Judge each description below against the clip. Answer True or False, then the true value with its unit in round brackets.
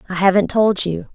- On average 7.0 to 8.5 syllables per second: False (5.3 syllables/s)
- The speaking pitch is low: False (190 Hz)